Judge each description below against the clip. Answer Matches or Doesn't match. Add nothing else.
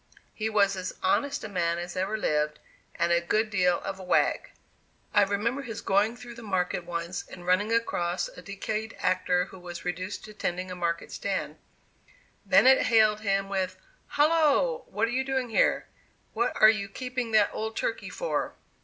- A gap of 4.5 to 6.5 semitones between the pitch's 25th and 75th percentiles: Doesn't match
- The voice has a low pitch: Doesn't match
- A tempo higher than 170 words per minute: Matches